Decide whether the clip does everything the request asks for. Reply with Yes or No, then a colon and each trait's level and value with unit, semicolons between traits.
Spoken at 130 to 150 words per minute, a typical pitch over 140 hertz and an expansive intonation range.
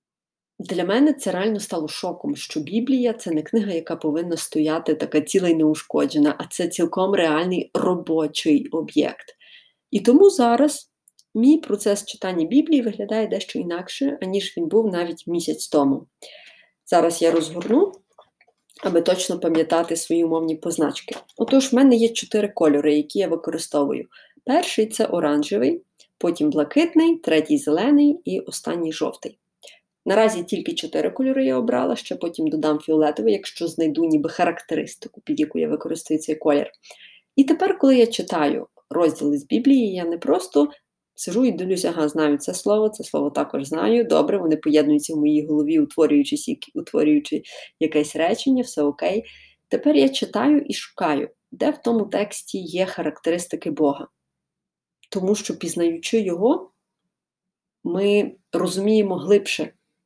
Yes: average, 140 wpm; medium, 185 Hz; wide, 7.1 semitones